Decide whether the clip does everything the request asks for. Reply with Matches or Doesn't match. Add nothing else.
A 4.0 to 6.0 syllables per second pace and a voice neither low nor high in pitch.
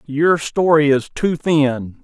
Doesn't match